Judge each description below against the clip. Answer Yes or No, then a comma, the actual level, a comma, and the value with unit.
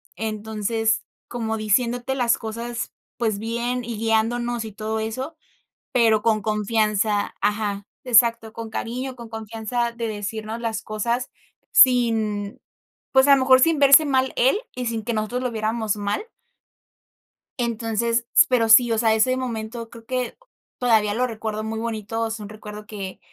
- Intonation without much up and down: Yes, narrow, 1.8 semitones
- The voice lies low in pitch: No, high, 225 Hz